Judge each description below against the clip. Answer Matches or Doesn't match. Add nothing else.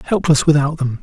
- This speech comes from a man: Matches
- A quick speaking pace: Doesn't match